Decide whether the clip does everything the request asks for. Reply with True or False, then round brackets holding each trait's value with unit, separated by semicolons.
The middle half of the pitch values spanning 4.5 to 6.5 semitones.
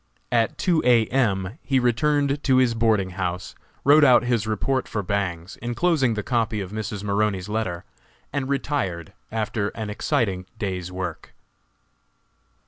True (5.0 semitones)